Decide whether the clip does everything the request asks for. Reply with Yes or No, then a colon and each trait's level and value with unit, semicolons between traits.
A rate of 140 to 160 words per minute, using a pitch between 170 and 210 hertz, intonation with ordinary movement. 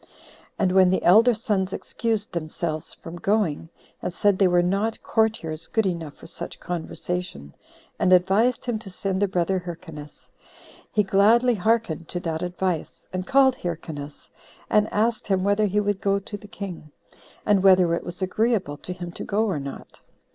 No: average, 170 wpm; high, 190 Hz; average, 3.4 semitones